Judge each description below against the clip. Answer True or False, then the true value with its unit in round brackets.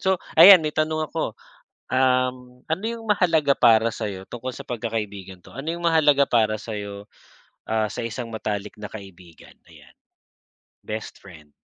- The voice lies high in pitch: False (115 Hz)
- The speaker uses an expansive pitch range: True (6.4 semitones)